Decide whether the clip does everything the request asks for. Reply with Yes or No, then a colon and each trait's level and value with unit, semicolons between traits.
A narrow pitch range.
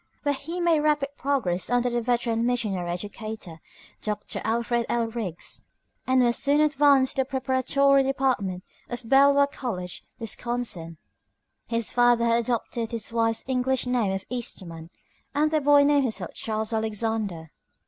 No: average, 3.7 semitones